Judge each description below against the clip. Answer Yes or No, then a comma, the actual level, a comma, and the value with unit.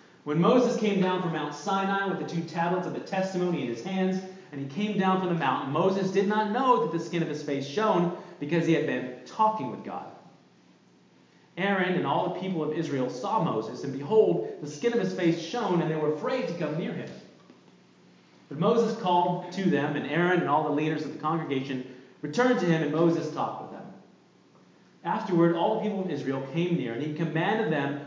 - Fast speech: Yes, fast, 215 wpm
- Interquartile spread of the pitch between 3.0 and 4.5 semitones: Yes, average, 4.1 semitones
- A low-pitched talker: No, medium, 170 Hz